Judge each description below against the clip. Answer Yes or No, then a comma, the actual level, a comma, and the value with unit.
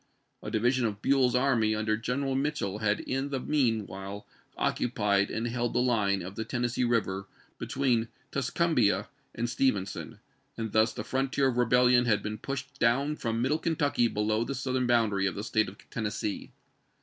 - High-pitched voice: No, low, 120 Hz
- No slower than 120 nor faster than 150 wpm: No, average, 175 wpm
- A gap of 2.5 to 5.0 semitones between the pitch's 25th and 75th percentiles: Yes, average, 3.6 semitones